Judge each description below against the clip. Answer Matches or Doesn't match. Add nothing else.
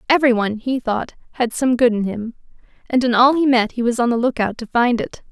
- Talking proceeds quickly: Matches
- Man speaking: Doesn't match